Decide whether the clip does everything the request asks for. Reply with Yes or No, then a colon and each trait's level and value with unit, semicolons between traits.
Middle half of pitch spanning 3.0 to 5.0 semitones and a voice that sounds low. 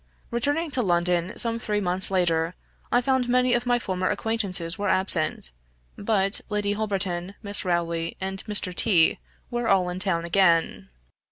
No: average, 4.4 semitones; high, 195 Hz